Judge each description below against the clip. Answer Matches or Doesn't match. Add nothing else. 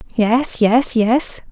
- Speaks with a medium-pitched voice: Doesn't match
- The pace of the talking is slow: Matches